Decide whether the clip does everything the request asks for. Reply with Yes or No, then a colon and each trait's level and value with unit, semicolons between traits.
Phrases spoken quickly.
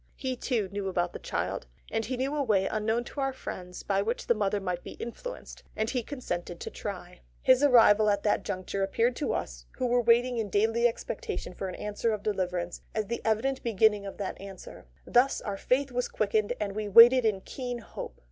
Yes: fast, 215 wpm